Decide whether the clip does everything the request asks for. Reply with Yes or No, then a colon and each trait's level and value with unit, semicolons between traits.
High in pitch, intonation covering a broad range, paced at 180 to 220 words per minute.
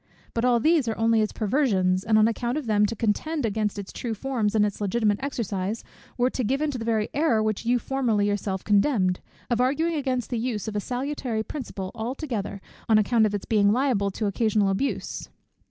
No: high, 225 Hz; average, 3.5 semitones; average, 200 wpm